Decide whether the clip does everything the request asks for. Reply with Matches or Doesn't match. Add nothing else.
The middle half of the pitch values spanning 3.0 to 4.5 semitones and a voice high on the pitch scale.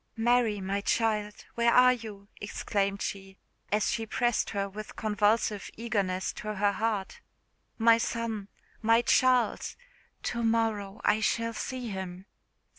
Doesn't match